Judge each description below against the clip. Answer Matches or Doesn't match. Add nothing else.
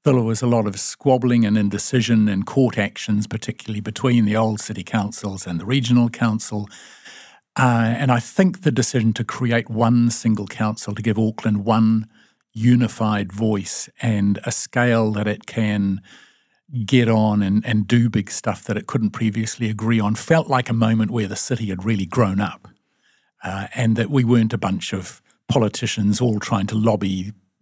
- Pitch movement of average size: Doesn't match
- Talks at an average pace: Matches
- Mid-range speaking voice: Doesn't match